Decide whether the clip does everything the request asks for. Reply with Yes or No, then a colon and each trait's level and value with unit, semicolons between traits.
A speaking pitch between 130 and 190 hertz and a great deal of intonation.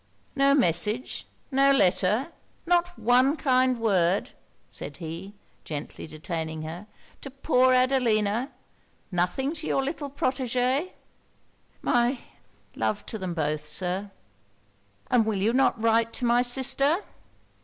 No: high, 240 Hz; wide, 6.4 semitones